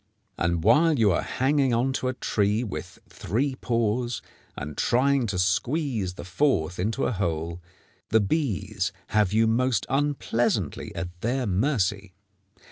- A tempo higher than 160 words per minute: No, average, 140 wpm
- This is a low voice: Yes, low, 110 Hz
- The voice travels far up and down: Yes, wide, 5.9 semitones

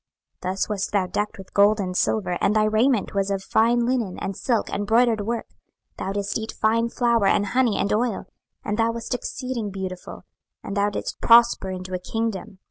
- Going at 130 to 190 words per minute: No, average, 200 wpm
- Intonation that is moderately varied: Yes, average, 3.0 semitones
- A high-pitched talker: Yes, high, 210 Hz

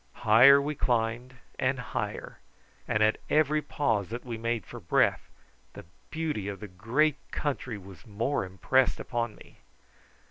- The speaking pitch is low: Yes, low, 120 Hz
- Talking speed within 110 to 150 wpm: Yes, average, 145 wpm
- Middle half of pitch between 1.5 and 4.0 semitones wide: No, average, 4.5 semitones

